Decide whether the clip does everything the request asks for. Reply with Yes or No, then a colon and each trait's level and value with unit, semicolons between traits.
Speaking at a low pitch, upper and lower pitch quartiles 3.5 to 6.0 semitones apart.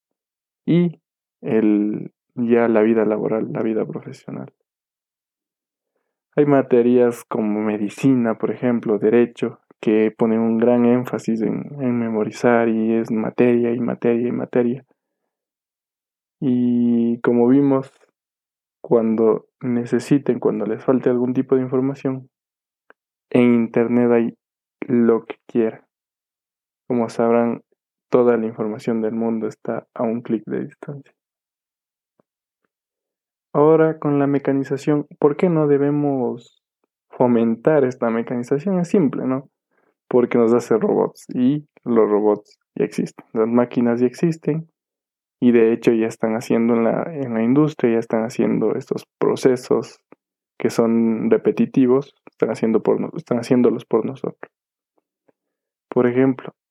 No: low, 120 Hz; average, 2.7 semitones